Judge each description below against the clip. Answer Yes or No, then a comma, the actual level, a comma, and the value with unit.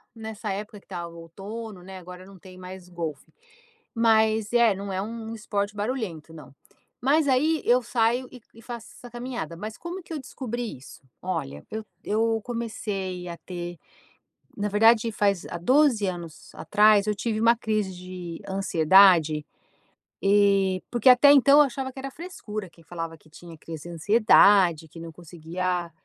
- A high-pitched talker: Yes, high, 205 Hz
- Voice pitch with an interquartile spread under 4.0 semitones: No, average, 4.7 semitones